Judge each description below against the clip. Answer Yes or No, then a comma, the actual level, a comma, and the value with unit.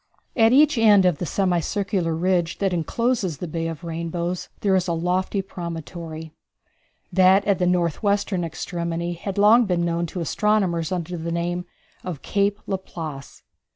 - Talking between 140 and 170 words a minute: Yes, average, 160 wpm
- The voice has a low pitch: No, medium, 180 Hz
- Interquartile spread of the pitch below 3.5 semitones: Yes, average, 2.7 semitones